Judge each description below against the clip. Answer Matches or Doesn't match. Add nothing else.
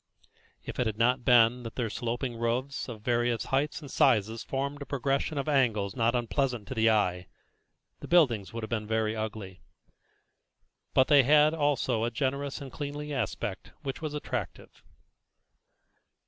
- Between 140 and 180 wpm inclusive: Matches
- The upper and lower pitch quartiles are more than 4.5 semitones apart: Doesn't match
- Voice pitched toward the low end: Matches